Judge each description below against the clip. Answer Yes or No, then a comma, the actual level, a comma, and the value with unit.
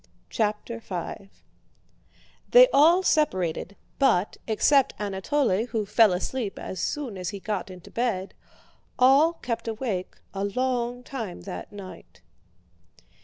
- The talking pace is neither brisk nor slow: No, slow, 120 wpm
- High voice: Yes, high, 220 Hz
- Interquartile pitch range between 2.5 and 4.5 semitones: No, average, 5.1 semitones